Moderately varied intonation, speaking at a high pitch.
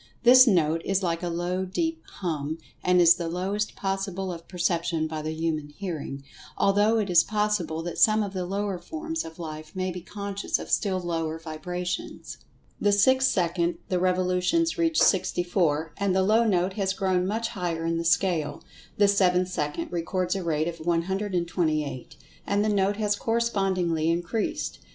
No: average, 3.2 semitones; medium, 180 Hz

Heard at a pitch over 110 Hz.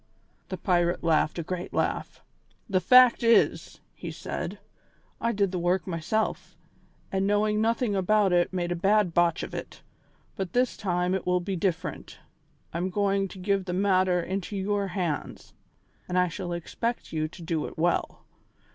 Yes: medium, 185 Hz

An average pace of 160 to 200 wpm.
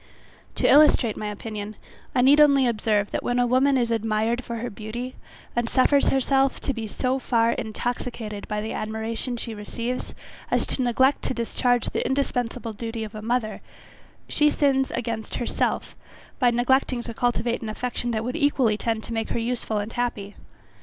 Yes: average, 175 wpm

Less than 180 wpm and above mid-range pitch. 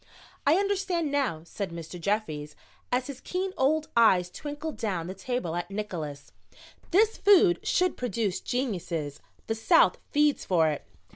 Yes: average, 145 wpm; high, 225 Hz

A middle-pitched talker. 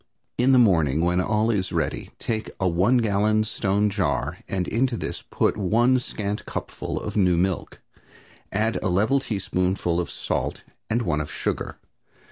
No: low, 100 Hz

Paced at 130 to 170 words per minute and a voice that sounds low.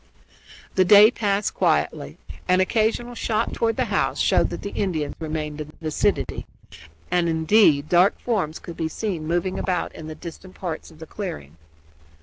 No: average, 165 wpm; medium, 175 Hz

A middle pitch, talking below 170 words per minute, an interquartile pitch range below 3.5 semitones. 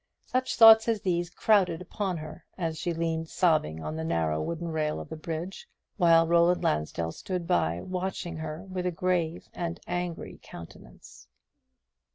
Yes: medium, 170 Hz; average, 160 wpm; average, 2.8 semitones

